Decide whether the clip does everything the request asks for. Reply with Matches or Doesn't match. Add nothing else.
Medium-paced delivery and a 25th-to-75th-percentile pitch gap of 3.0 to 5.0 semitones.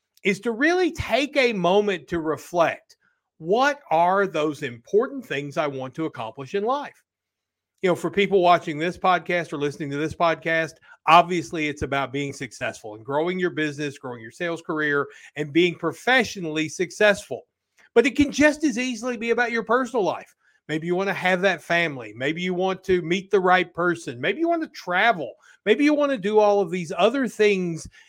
Doesn't match